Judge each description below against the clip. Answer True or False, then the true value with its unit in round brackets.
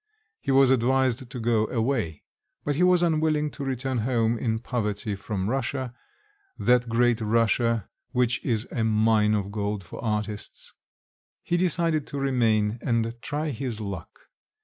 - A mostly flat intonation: False (3.6 semitones)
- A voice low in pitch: True (120 Hz)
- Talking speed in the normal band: True (150 wpm)